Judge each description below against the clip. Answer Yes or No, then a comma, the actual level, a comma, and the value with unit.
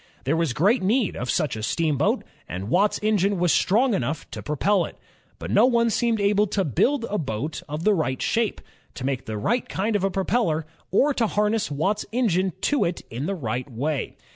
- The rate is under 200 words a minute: No, fast, 205 wpm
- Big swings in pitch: Yes, wide, 6.5 semitones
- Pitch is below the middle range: No, high, 190 Hz